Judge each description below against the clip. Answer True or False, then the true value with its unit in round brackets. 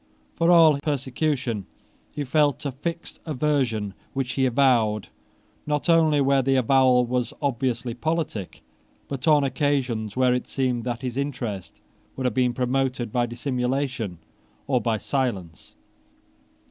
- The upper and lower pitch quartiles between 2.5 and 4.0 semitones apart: True (2.8 semitones)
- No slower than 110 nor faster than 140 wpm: True (135 wpm)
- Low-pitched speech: True (130 Hz)